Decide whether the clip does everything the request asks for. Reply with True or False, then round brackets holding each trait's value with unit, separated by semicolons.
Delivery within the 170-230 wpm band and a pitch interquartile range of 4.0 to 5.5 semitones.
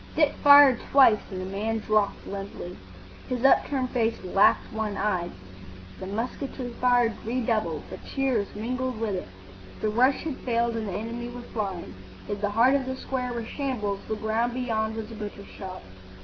False (175 wpm; 3.4 semitones)